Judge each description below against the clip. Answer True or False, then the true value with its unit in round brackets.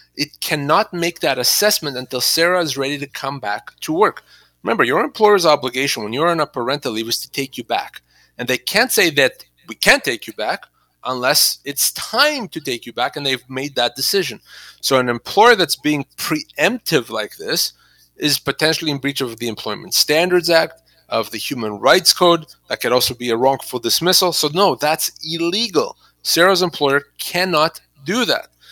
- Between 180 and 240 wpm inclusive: True (185 wpm)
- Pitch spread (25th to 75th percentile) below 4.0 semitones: False (4.6 semitones)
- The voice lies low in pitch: False (150 Hz)